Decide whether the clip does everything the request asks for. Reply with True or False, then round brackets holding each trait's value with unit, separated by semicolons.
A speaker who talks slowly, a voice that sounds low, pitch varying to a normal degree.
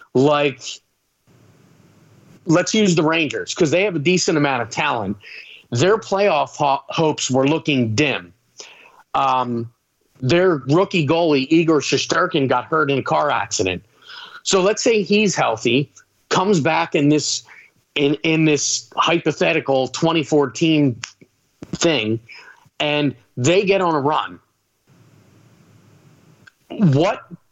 False (120 wpm; 150 Hz; 4.4 semitones)